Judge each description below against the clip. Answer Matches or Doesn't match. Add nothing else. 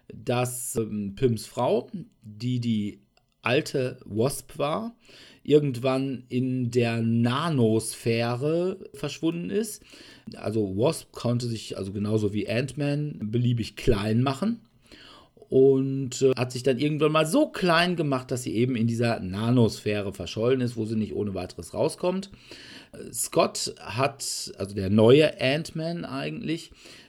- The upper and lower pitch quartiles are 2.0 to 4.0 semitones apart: Doesn't match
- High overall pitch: Doesn't match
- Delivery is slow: Matches